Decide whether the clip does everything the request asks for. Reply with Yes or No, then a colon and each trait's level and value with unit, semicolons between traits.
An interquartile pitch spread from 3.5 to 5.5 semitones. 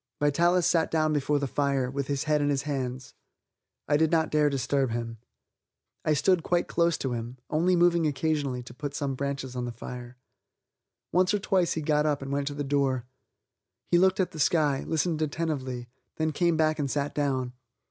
No: average, 3.1 semitones